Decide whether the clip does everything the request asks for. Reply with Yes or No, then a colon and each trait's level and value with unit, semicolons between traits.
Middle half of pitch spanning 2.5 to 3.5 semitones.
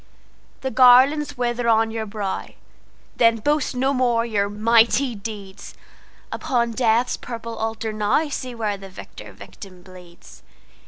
Yes: average, 2.9 semitones